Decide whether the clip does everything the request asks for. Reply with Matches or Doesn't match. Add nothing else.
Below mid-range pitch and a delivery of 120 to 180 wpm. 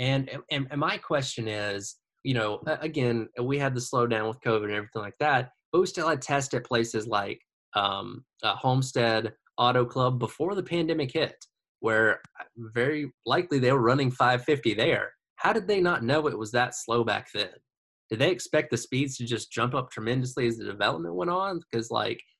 Doesn't match